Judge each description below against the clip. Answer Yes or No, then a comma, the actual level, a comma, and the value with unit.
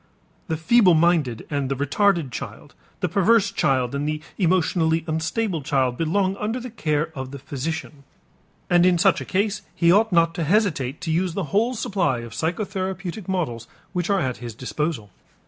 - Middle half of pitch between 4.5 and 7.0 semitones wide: Yes, average, 5.2 semitones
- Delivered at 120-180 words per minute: Yes, average, 175 wpm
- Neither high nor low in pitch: Yes, medium, 165 Hz